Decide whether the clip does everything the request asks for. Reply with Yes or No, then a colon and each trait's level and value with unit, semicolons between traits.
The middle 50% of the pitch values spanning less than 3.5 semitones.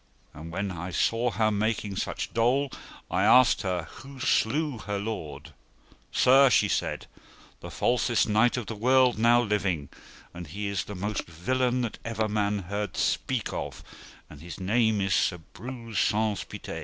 No: average, 3.8 semitones